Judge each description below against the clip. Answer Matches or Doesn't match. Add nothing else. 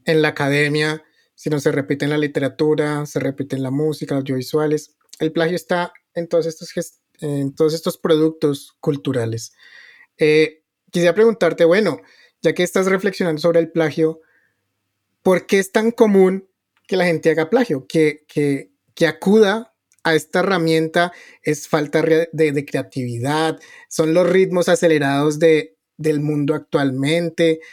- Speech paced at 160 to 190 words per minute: Doesn't match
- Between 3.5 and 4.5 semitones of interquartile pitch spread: Doesn't match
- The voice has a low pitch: Doesn't match